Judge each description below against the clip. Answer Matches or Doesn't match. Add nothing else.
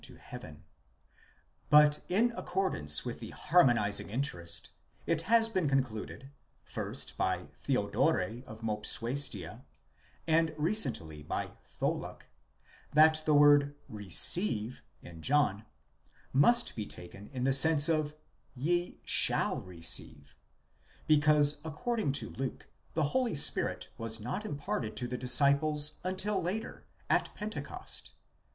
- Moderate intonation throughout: Doesn't match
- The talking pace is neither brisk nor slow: Doesn't match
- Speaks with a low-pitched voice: Doesn't match